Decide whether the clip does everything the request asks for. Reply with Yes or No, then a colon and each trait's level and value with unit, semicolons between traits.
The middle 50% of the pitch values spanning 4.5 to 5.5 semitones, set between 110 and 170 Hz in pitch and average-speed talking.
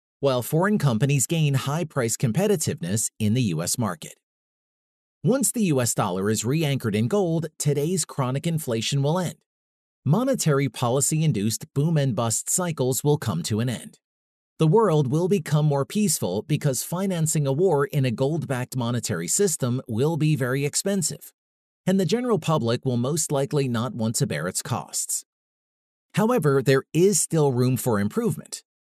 Yes: average, 4.9 semitones; medium, 140 Hz; average, 160 wpm